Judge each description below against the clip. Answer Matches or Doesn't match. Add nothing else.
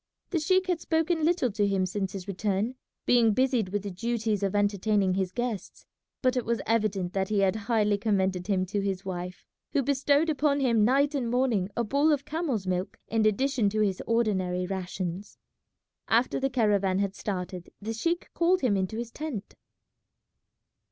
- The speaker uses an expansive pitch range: Doesn't match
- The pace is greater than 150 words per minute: Matches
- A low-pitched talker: Doesn't match